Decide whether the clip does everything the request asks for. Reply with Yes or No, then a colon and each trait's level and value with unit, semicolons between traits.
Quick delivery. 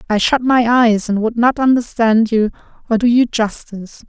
No: average, 190 wpm